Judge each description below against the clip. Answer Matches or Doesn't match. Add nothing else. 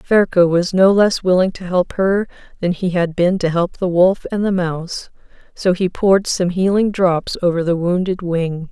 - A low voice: Doesn't match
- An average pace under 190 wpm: Doesn't match